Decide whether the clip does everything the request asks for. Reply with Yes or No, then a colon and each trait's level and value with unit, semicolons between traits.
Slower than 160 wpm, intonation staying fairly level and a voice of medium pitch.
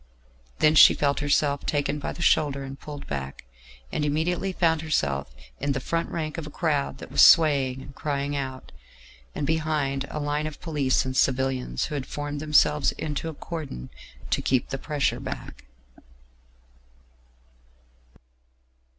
Yes: average, 150 wpm; narrow, 2.3 semitones; medium, 145 Hz